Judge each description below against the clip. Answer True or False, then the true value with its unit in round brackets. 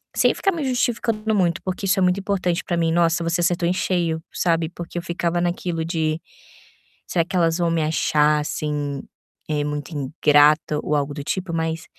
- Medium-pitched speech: True (170 Hz)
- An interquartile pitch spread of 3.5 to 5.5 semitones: False (2.7 semitones)